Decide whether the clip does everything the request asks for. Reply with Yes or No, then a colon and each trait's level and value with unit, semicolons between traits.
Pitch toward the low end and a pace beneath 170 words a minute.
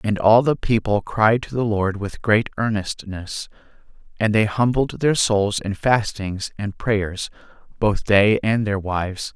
Yes: low, 105 Hz; average, 160 wpm